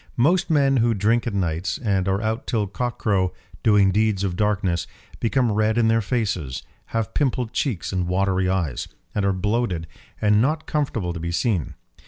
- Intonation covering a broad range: No, average, 4.0 semitones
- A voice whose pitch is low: Yes, low, 105 Hz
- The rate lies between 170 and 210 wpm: Yes, average, 175 wpm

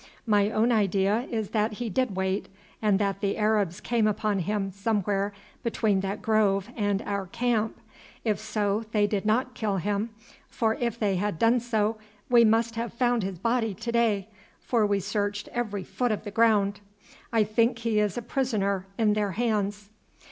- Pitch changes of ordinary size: No, narrow, 2.2 semitones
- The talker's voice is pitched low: No, high, 210 Hz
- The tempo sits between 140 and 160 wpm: No, average, 180 wpm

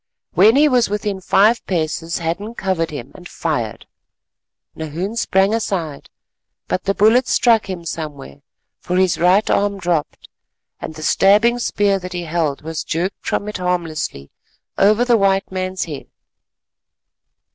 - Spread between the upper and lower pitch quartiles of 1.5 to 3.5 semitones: No, average, 4.0 semitones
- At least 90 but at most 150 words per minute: Yes, average, 145 wpm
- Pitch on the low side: No, medium, 185 Hz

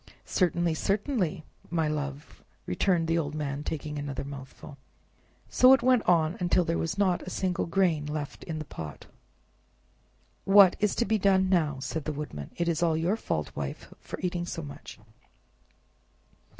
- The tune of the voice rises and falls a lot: No, average, 3.9 semitones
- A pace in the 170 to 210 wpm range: No, average, 160 wpm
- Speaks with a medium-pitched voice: Yes, medium, 165 Hz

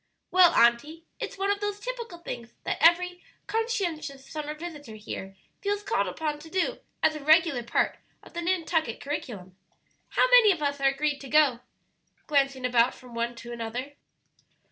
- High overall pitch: Yes, very high, 300 Hz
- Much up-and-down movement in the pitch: Yes, wide, 6.0 semitones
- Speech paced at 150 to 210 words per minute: Yes, average, 165 wpm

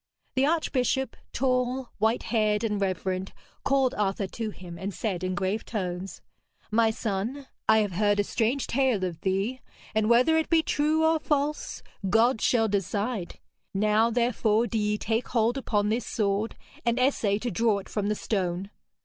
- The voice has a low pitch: No, high, 220 Hz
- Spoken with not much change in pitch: No, average, 3.8 semitones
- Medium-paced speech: Yes, average, 165 wpm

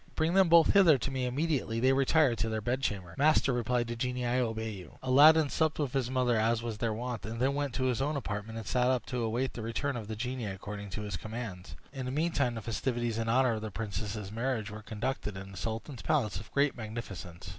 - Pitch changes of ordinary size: Yes, average, 3.5 semitones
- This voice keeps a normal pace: No, fast, 235 wpm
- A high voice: No, low, 120 Hz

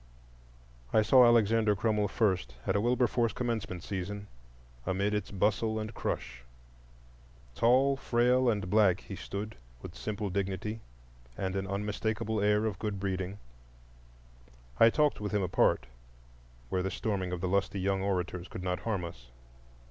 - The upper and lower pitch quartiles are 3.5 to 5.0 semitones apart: No, average, 2.7 semitones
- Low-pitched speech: Yes, low, 105 Hz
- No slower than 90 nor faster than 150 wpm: Yes, average, 145 wpm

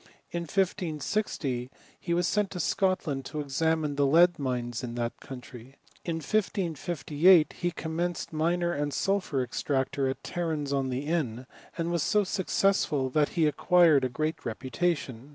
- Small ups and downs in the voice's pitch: No, average, 4.6 semitones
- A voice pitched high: No, medium, 155 Hz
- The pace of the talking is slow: No, average, 150 wpm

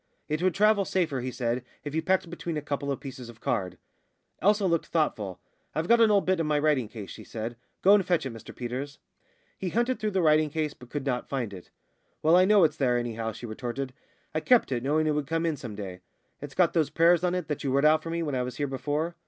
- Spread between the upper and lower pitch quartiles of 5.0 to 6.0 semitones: Yes, average, 5.3 semitones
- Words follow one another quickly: Yes, fast, 260 wpm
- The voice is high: No, medium, 150 Hz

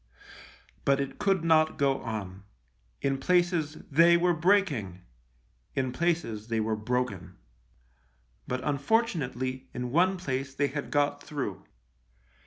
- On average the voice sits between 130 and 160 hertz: Yes, medium, 140 Hz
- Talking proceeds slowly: Yes, slow, 120 wpm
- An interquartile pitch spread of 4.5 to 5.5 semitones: Yes, average, 5.2 semitones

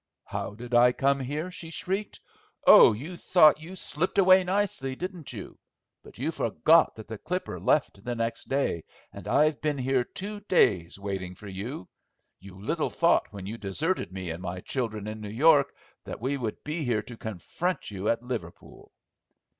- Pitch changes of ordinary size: No, wide, 7.6 semitones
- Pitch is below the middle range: Yes, low, 125 Hz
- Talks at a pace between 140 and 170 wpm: No, average, 180 wpm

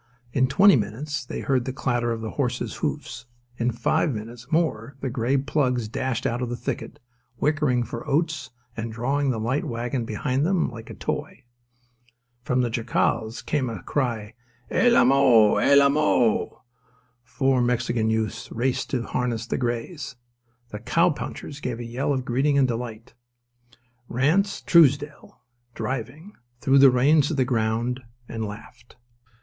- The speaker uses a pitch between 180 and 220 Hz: No, low, 125 Hz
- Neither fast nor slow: Yes, average, 155 wpm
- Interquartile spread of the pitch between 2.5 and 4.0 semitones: Yes, average, 3.2 semitones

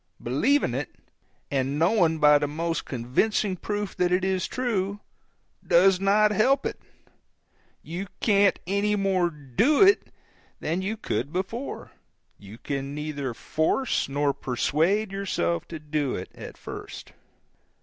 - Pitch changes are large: Yes, wide, 6.0 semitones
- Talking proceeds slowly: Yes, slow, 130 wpm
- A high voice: No, medium, 175 Hz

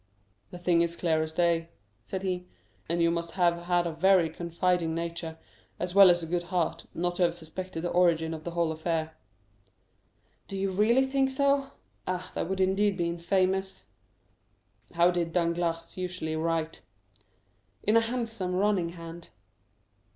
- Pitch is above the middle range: No, medium, 175 Hz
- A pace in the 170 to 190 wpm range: No, average, 160 wpm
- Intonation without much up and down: Yes, narrow, 2.0 semitones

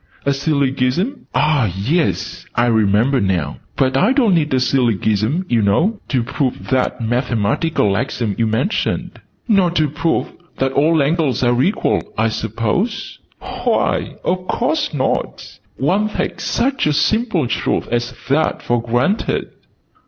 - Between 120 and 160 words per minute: Yes, average, 140 wpm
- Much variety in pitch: Yes, wide, 6.2 semitones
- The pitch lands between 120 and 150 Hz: Yes, low, 135 Hz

